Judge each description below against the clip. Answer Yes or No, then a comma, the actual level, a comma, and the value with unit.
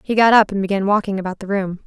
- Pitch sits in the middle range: No, high, 200 Hz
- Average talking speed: No, fast, 290 wpm